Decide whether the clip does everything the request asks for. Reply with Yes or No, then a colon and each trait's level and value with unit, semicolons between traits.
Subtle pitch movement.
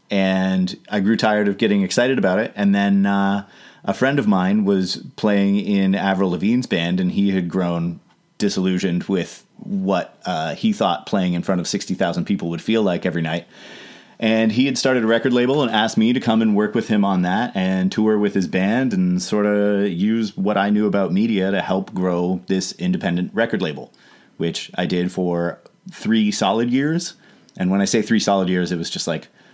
No: average, 5.3 semitones